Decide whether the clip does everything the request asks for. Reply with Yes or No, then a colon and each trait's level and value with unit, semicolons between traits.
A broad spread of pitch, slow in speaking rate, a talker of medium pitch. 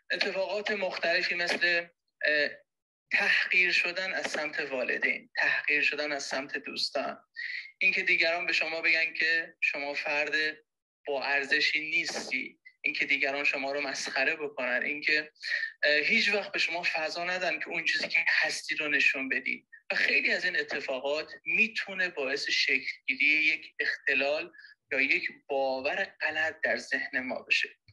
No: wide, 6.9 semitones; average, 135 wpm; medium, 175 Hz